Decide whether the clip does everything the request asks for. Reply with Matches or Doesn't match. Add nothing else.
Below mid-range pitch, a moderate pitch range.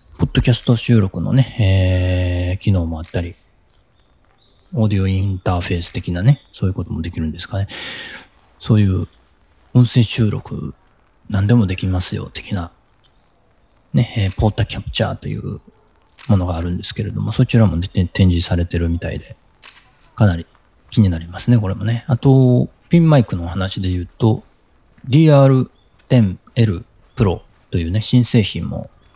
Matches